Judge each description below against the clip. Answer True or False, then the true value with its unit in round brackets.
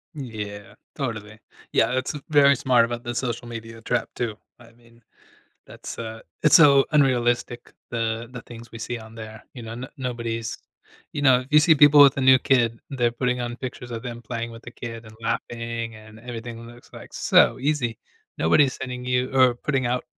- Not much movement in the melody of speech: True (2.0 semitones)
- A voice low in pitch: True (120 Hz)